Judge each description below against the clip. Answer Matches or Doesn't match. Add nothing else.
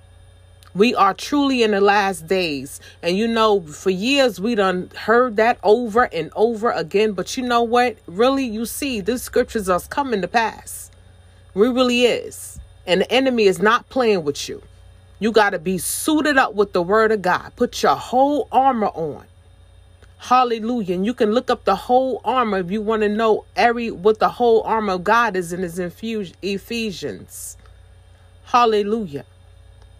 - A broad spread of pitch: Matches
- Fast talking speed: Doesn't match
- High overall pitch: Matches